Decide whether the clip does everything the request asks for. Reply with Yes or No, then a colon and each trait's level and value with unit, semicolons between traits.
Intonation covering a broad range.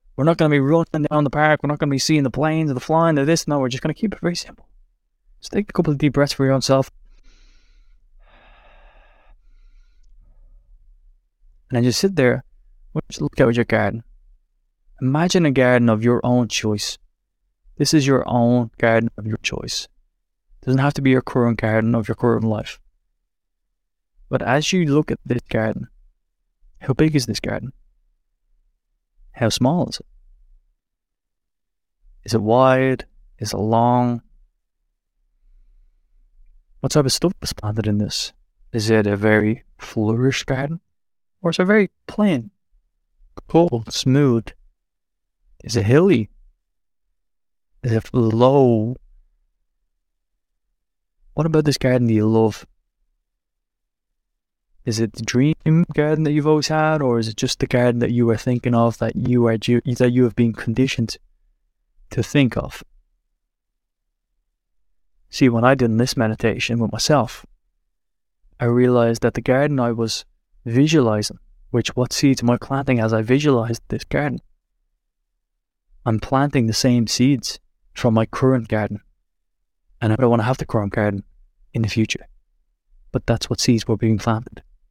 No: average, 3.8 semitones